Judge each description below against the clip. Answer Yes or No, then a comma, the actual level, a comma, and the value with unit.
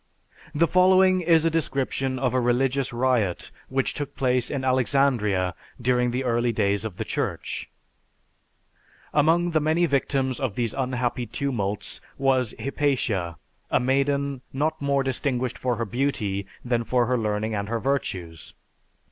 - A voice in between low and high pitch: No, low, 130 Hz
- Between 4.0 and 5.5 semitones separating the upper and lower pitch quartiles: No, average, 3.1 semitones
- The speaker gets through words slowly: No, average, 145 wpm